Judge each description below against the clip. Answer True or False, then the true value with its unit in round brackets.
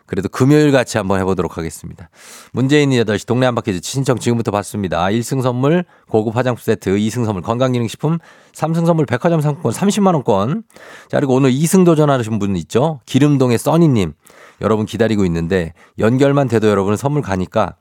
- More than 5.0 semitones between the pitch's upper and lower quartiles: True (5.5 semitones)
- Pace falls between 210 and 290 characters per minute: False (390 characters per minute)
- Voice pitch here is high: False (120 Hz)